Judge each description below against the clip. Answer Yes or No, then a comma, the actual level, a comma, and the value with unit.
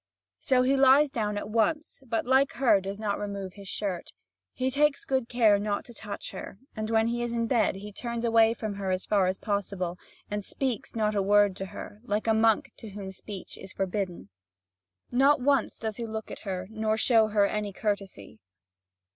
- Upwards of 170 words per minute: Yes, fast, 205 wpm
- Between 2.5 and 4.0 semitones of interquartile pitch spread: Yes, average, 2.8 semitones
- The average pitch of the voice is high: Yes, high, 215 Hz